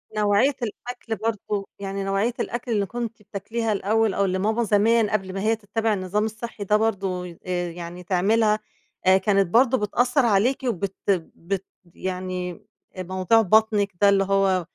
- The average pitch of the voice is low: No, high, 205 Hz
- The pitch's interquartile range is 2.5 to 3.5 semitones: Yes, average, 2.8 semitones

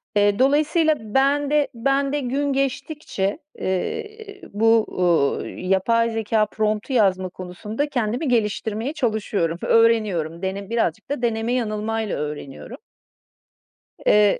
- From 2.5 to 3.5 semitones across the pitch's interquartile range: No, wide, 5.4 semitones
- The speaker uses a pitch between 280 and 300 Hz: No, high, 225 Hz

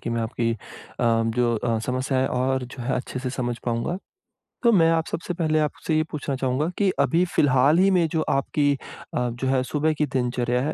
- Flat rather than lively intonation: No, average, 4.1 semitones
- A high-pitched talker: No, low, 135 Hz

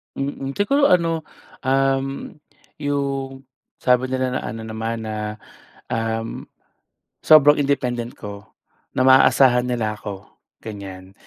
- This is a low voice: Yes, low, 130 Hz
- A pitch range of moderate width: Yes, average, 3.5 semitones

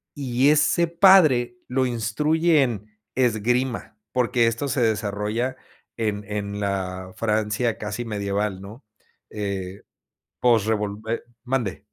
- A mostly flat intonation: No, average, 3.7 semitones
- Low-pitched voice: Yes, low, 115 Hz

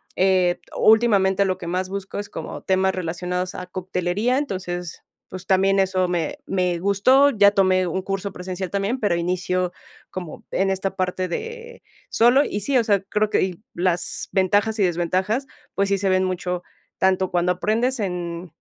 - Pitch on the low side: No, high, 190 Hz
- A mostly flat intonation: Yes, narrow, 1.9 semitones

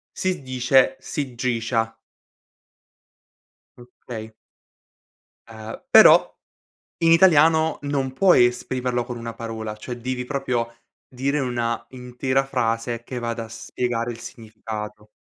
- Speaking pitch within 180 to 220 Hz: No, low, 125 Hz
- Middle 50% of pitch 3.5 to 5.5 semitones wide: No, narrow, 2.4 semitones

